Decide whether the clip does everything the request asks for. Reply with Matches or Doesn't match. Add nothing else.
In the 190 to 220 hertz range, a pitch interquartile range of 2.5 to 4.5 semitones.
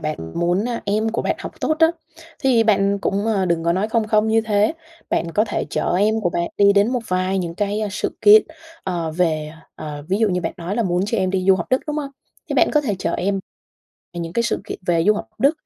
Matches